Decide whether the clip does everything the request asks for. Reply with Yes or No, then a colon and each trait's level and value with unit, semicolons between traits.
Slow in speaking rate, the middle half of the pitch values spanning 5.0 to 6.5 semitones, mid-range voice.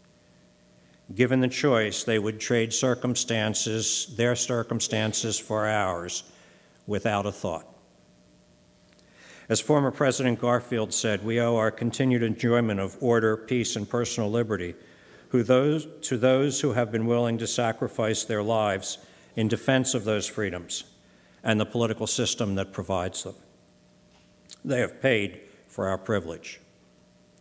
No: slow, 125 wpm; wide, 5.4 semitones; low, 110 Hz